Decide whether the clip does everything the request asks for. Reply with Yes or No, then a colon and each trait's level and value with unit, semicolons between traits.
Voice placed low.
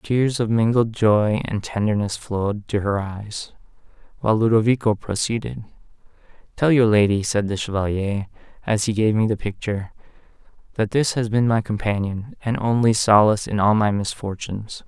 Yes: low, 110 Hz